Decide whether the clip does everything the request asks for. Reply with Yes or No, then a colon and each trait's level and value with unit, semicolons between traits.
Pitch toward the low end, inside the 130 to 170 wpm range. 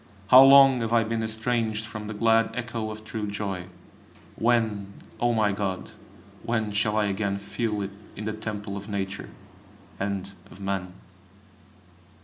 Yes: low, 110 Hz; average, 150 wpm